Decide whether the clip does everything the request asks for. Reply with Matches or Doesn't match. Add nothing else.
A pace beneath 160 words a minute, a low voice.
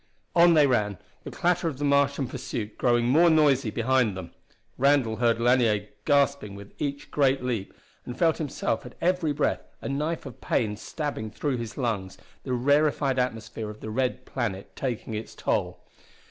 Doesn't match